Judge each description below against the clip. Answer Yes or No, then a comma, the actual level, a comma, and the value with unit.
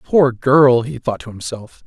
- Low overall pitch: Yes, low, 125 Hz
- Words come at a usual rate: Yes, average, 195 wpm